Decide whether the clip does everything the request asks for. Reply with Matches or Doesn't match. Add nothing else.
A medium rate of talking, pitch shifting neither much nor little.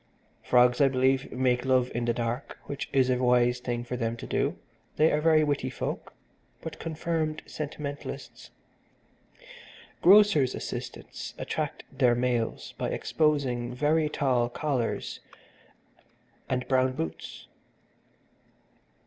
Doesn't match